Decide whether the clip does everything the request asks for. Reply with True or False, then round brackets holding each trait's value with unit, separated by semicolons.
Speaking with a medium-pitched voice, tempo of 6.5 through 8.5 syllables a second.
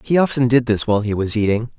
False (120 Hz; 6.7 syllables/s)